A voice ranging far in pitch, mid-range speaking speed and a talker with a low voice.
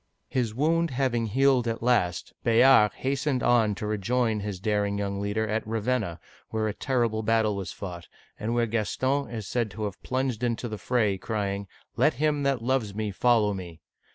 No: average, 3.3 semitones; average, 180 wpm; low, 110 Hz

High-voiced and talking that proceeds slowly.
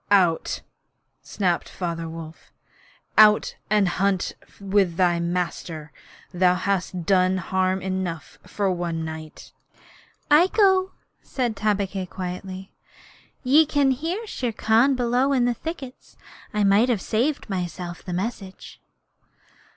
Yes: high, 195 Hz; slow, 120 wpm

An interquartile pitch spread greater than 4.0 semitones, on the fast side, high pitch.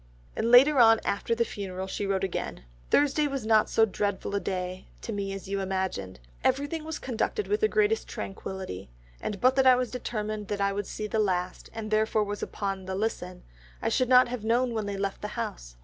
Yes: average, 4.4 semitones; fast, 210 wpm; high, 210 Hz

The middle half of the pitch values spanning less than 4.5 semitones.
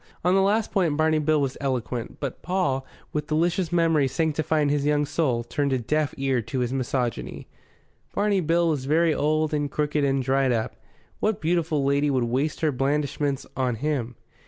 Yes: average, 3.0 semitones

